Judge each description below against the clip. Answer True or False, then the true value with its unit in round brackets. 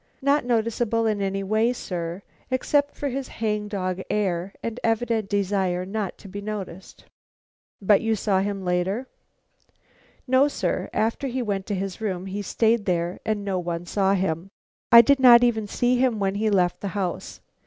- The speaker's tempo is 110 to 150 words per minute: False (175 wpm)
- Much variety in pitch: False (3.3 semitones)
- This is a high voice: True (205 Hz)